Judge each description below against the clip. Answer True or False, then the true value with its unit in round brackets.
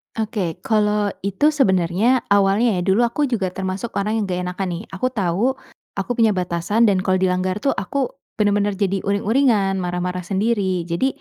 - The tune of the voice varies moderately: True (3.4 semitones)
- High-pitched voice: True (200 Hz)